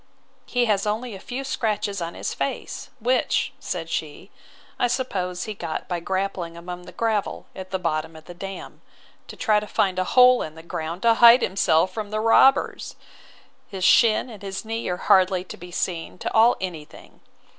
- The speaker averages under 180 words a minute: No, average, 190 wpm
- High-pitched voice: Yes, high, 195 Hz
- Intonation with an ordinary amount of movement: Yes, average, 4.1 semitones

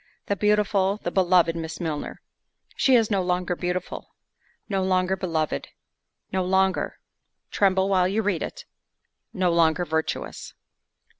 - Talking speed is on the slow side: Yes, slow, 95 wpm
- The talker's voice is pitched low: No, medium, 185 Hz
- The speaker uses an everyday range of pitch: No, narrow, 2.1 semitones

